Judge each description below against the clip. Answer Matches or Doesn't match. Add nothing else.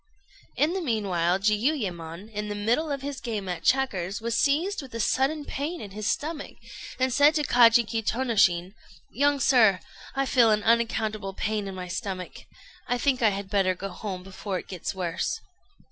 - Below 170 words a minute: Doesn't match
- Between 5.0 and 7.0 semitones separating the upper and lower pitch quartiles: Matches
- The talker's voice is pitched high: Matches